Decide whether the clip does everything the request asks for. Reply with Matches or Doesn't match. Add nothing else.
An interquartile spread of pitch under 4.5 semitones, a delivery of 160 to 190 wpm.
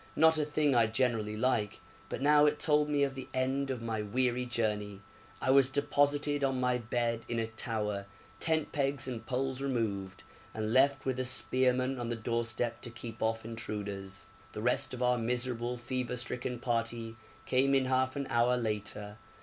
Matches